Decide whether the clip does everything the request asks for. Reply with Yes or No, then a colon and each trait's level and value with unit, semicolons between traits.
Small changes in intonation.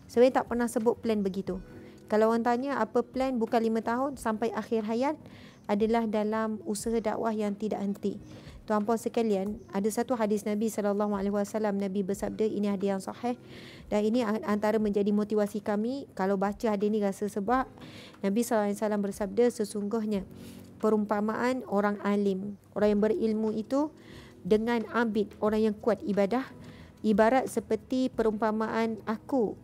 Yes: narrow, 1.9 semitones